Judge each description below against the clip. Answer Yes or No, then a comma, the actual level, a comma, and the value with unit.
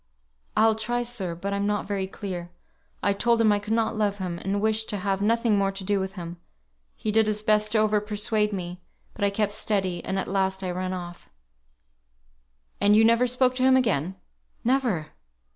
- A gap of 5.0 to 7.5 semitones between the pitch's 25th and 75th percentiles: No, narrow, 2.5 semitones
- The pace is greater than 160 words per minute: Yes, average, 200 wpm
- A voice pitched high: Yes, high, 205 Hz